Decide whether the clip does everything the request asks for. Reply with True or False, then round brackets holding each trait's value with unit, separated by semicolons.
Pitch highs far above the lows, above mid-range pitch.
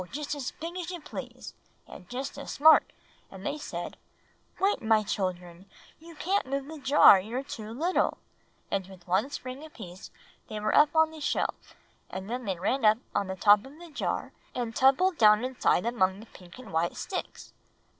True (7.1 semitones; 245 Hz)